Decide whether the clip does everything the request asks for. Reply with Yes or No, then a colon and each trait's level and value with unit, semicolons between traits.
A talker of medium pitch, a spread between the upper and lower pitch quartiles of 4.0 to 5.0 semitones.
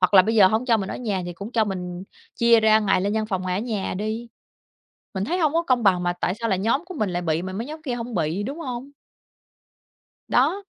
No: high, 215 Hz; average, 4.3 semitones